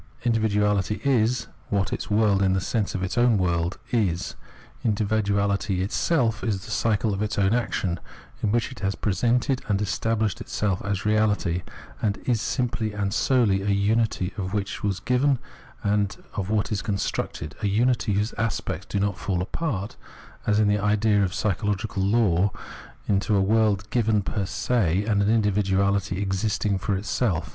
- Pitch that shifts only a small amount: Yes, narrow, 2.2 semitones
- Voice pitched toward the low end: Yes, low, 105 Hz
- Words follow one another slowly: No, average, 165 wpm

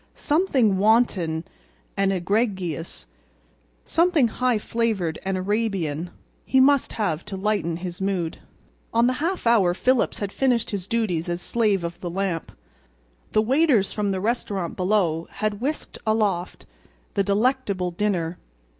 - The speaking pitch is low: No, high, 200 Hz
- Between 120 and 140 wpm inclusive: Yes, slow, 135 wpm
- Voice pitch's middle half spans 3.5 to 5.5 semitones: Yes, average, 4.6 semitones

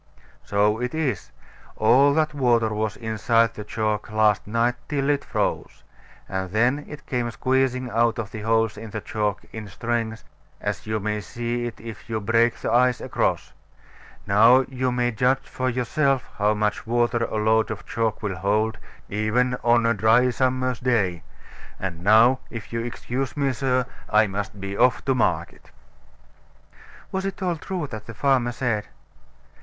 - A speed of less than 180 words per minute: Yes, average, 165 wpm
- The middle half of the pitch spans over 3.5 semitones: No, average, 2.9 semitones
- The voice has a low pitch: Yes, low, 115 Hz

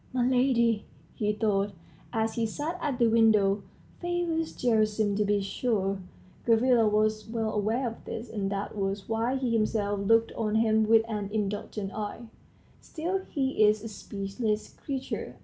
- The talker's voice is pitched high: Yes, high, 220 Hz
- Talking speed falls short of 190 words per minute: Yes, average, 155 wpm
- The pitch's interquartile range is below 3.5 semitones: Yes, narrow, 2.5 semitones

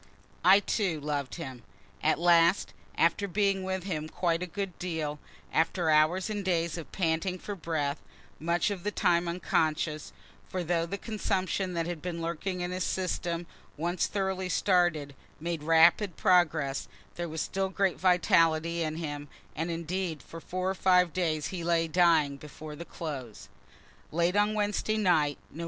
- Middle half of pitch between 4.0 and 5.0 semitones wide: No, narrow, 2.6 semitones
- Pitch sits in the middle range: Yes, medium, 170 Hz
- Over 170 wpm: No, average, 160 wpm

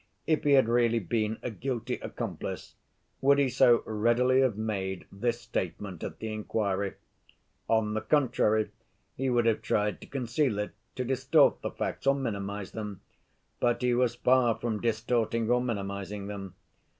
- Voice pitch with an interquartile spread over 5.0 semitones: No, average, 3.2 semitones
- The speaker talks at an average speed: Yes, average, 160 wpm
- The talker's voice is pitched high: No, low, 115 Hz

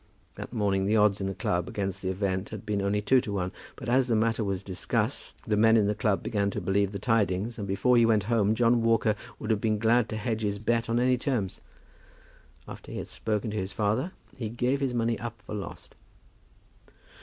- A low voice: Yes, low, 105 Hz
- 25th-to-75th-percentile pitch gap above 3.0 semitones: No, narrow, 2.6 semitones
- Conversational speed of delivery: No, fast, 225 wpm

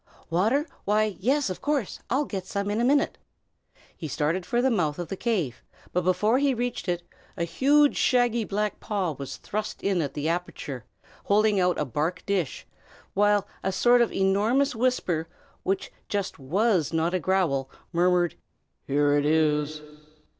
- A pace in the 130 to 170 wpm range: Yes, average, 165 wpm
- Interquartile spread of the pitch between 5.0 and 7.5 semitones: Yes, wide, 5.6 semitones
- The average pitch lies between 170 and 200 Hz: Yes, high, 190 Hz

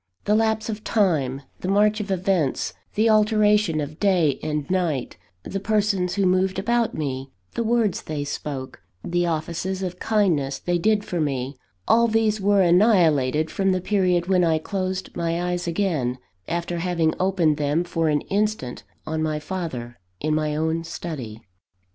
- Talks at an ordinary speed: Yes, average, 160 wpm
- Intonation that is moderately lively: Yes, average, 4.6 semitones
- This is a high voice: No, medium, 175 Hz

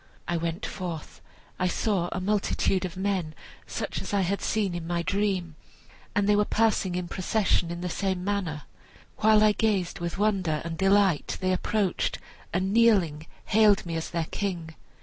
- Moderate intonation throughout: Yes, average, 3.0 semitones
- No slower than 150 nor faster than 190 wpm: Yes, average, 170 wpm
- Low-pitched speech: No, medium, 185 Hz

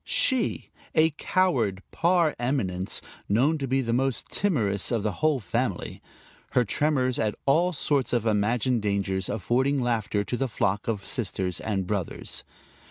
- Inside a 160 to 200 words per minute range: No, average, 150 wpm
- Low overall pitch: Yes, low, 120 Hz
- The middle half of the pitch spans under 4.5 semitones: No, wide, 5.4 semitones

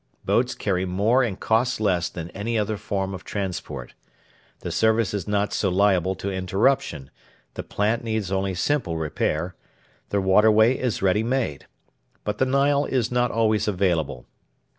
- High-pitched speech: No, low, 105 Hz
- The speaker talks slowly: No, average, 155 wpm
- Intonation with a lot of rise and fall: No, average, 3.6 semitones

